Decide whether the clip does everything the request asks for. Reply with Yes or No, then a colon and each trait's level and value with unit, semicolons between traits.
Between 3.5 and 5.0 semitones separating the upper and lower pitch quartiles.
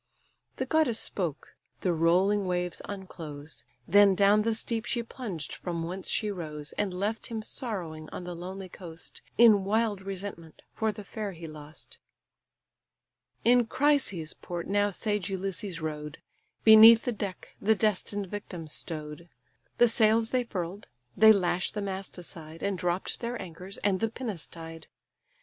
Yes: average, 4.2 semitones